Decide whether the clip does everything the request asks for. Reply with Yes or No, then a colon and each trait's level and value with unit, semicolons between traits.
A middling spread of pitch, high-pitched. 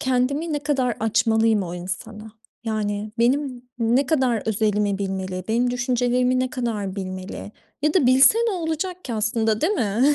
Yes: average, 3.8 semitones; high, 235 Hz